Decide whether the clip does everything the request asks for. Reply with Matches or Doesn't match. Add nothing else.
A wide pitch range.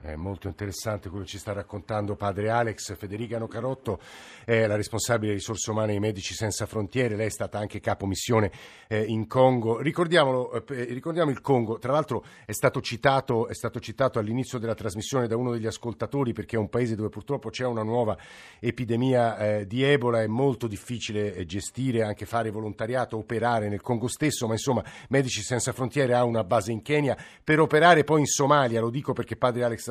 Doesn't match